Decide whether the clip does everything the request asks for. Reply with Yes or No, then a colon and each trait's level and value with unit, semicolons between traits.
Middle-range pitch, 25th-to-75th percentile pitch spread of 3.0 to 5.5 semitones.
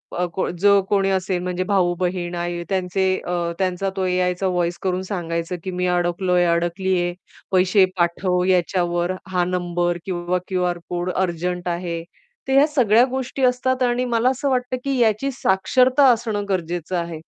No: medium, 180 Hz; narrow, 2.5 semitones